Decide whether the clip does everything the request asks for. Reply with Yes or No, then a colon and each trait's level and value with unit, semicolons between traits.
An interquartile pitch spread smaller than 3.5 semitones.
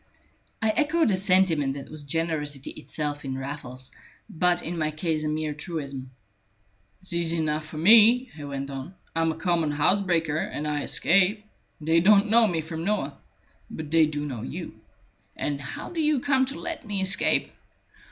No: average, 4.7 semitones